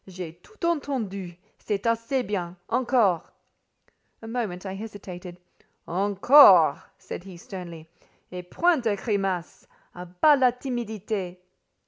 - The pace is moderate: No, slow, 115 wpm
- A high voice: Yes, high, 200 Hz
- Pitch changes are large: No, average, 5.0 semitones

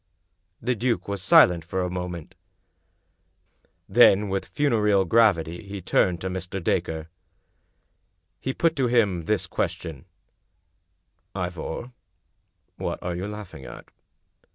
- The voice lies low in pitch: Yes, very low, 95 Hz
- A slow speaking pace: Yes, slow, 120 wpm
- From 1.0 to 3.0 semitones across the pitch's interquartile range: No, average, 3.8 semitones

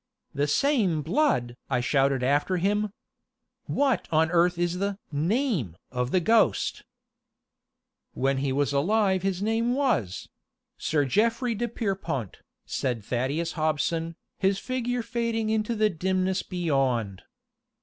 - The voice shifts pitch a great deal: Yes, wide, 7.7 semitones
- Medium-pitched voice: Yes, medium, 180 Hz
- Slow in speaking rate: Yes, slow, 125 wpm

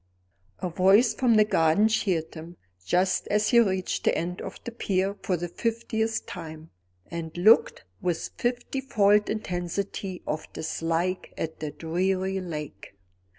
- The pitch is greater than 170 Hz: Yes, medium, 185 Hz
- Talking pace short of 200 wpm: Yes, average, 145 wpm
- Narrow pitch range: No, average, 4.3 semitones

